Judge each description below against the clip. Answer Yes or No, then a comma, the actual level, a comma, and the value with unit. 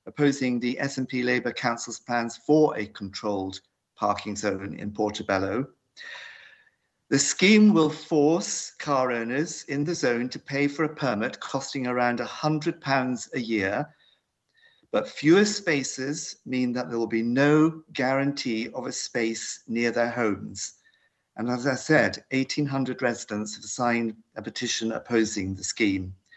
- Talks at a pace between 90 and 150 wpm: Yes, average, 140 wpm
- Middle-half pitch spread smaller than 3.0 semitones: No, average, 4.7 semitones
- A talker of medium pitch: No, low, 125 Hz